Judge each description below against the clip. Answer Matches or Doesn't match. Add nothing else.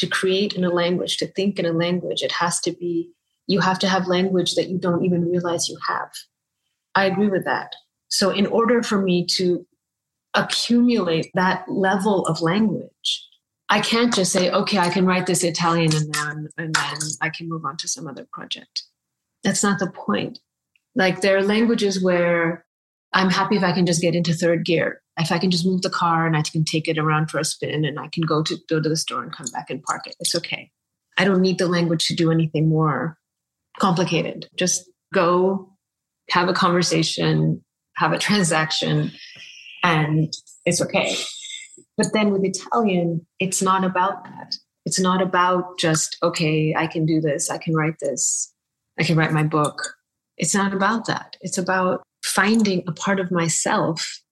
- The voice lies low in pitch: Doesn't match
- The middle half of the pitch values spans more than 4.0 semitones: Doesn't match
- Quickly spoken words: Matches